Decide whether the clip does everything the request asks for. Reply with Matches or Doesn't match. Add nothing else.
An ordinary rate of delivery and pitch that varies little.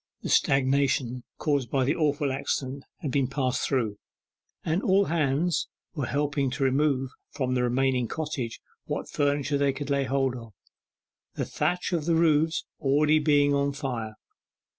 Matches